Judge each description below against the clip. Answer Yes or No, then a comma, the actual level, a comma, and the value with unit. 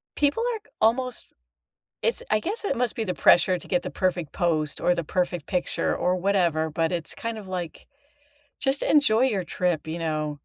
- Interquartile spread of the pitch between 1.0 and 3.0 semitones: No, wide, 5.4 semitones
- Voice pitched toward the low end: No, medium, 180 Hz